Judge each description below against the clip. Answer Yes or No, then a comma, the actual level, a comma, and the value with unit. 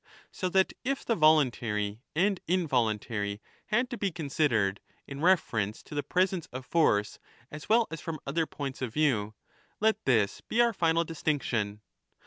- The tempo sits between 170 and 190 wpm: No, average, 160 wpm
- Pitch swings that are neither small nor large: No, wide, 8.2 semitones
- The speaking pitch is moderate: Yes, medium, 150 Hz